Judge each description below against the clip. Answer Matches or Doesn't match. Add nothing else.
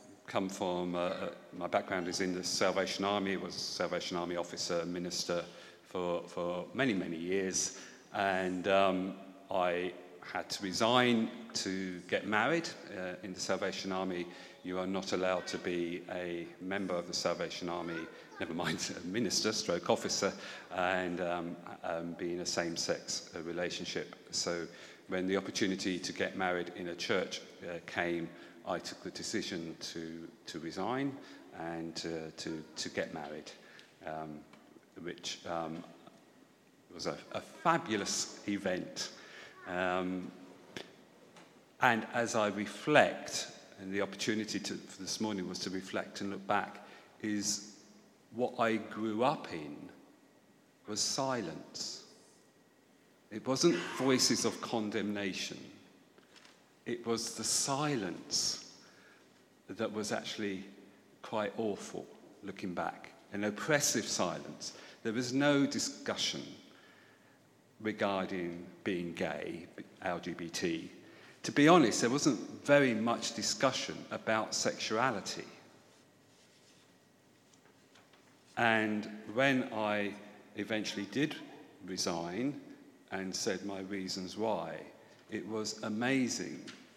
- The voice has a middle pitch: Doesn't match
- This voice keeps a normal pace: Doesn't match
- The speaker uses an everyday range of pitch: Matches